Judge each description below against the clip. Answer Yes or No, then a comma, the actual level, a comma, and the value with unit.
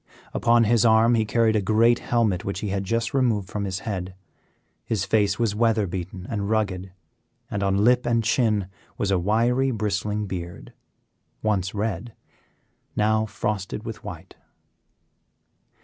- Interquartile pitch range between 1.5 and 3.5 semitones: Yes, average, 2.8 semitones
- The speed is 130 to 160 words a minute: Yes, average, 150 wpm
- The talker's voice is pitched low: Yes, low, 105 Hz